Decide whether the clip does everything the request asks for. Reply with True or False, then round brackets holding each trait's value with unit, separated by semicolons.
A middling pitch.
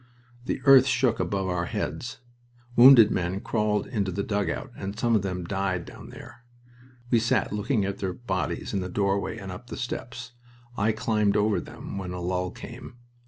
False (100 Hz)